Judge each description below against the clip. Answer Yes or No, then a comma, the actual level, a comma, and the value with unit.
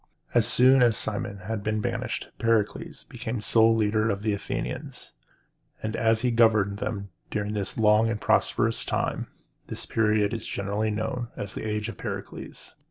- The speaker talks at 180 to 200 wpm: No, average, 165 wpm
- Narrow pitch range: Yes, narrow, 1.6 semitones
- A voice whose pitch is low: Yes, low, 110 Hz